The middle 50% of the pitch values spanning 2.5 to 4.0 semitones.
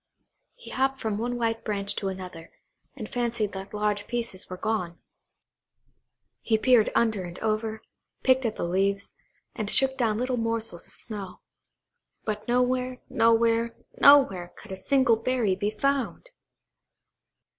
Yes: average, 3.5 semitones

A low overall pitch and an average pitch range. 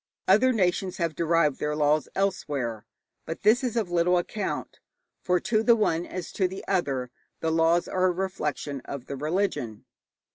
No: medium, 175 Hz; average, 4.3 semitones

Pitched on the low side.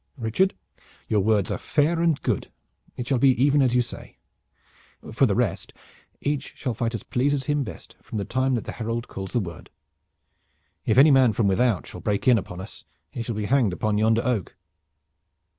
Yes: low, 120 Hz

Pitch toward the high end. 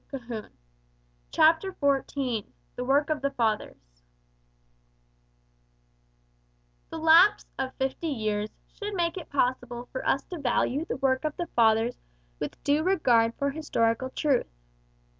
Yes: very high, 270 Hz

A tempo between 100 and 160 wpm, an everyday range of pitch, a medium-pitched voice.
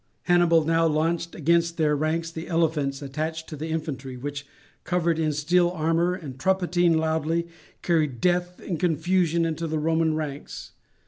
No: average, 150 wpm; narrow, 1.8 semitones; medium, 160 Hz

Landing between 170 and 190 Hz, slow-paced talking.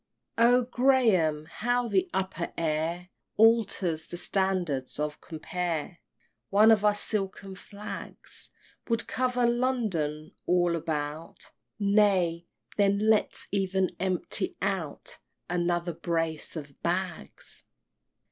Yes: medium, 185 Hz; slow, 105 wpm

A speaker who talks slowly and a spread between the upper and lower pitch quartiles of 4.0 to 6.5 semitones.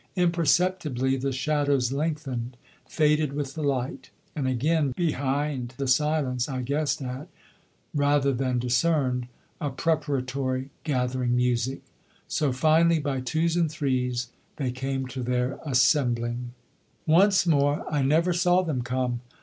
No: slow, 125 wpm; average, 3.3 semitones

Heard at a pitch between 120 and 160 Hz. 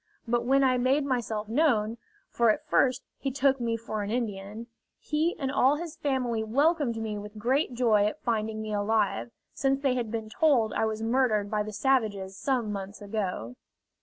No: high, 230 Hz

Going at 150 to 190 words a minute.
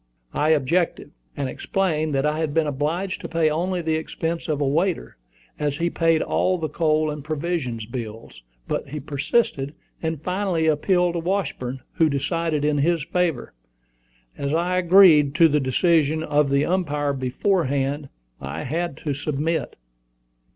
Yes: average, 155 wpm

